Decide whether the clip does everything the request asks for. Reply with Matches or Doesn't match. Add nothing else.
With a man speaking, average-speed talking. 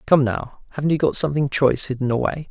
Doesn't match